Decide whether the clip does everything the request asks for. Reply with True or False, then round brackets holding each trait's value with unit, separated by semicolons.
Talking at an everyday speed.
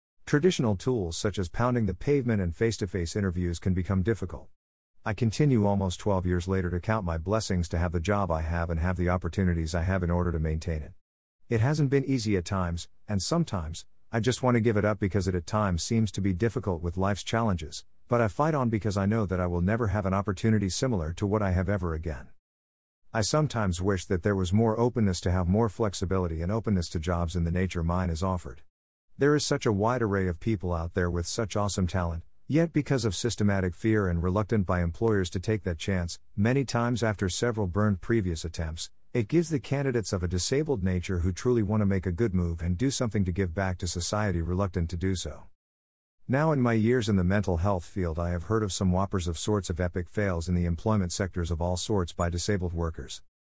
False (230 wpm)